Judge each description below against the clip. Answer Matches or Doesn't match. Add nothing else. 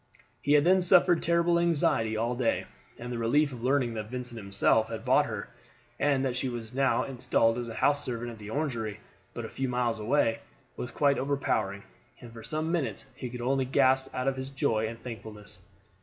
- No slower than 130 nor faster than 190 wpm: Doesn't match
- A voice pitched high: Doesn't match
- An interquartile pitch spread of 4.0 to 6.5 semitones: Doesn't match